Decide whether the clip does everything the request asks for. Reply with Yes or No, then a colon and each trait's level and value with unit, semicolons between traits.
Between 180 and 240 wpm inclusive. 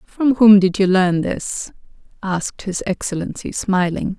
No: average, 145 wpm